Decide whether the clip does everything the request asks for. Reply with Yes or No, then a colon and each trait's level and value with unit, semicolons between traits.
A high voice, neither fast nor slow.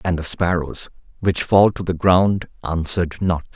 No: very low, 90 Hz; average, 170 wpm